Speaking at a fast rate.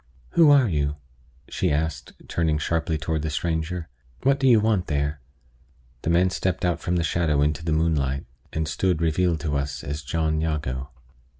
No: average, 175 wpm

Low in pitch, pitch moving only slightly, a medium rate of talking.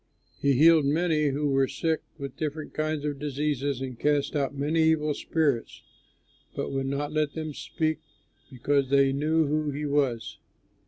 No: medium, 145 Hz; narrow, 1.9 semitones; average, 160 wpm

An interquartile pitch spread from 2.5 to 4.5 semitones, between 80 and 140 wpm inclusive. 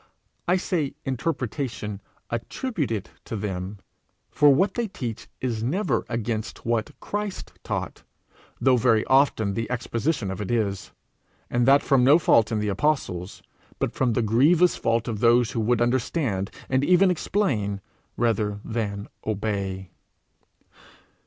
No: average, 4.9 semitones; slow, 135 wpm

